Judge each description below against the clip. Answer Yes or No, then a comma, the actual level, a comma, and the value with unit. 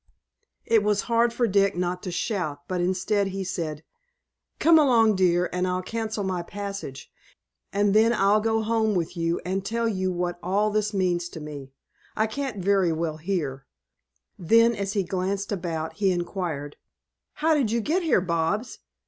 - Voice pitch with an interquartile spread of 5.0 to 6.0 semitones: No, average, 3.7 semitones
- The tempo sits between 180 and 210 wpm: No, average, 170 wpm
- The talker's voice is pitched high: Yes, high, 195 Hz